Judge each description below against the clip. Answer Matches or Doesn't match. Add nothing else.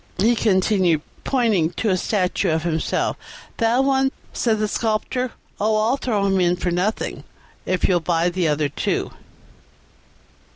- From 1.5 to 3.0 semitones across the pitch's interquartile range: Doesn't match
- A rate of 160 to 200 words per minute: Doesn't match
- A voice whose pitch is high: Matches